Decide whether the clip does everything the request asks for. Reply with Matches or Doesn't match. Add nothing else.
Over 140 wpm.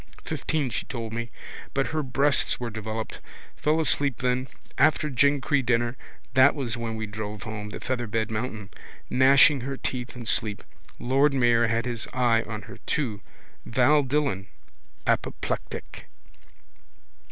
Doesn't match